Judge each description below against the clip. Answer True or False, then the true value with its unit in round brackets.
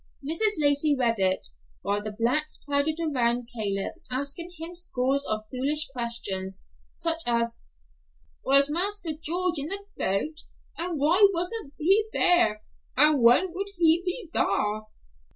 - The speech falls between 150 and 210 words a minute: False (135 wpm)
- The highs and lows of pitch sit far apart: True (6.5 semitones)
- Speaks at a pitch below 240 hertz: False (295 Hz)